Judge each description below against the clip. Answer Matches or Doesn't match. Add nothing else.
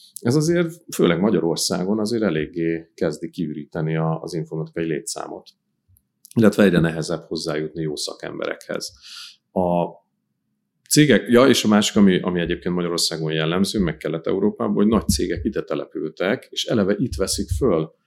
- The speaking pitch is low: Matches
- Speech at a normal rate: Matches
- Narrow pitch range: Doesn't match